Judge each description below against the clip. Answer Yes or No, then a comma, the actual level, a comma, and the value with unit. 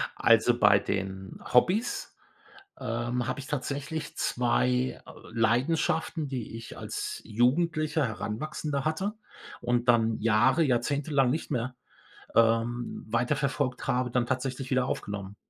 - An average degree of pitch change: Yes, average, 3.7 semitones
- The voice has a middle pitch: No, low, 125 Hz